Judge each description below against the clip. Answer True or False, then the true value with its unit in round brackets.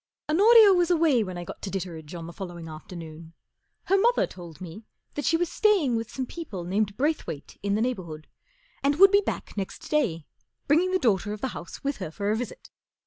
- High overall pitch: True (215 Hz)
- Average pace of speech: False (220 wpm)